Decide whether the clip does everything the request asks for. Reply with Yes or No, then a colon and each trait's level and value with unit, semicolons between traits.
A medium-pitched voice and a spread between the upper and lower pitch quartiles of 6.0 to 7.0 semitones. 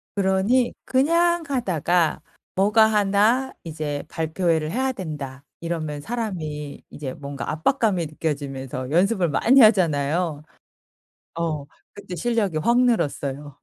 Yes: medium, 170 Hz; wide, 6.7 semitones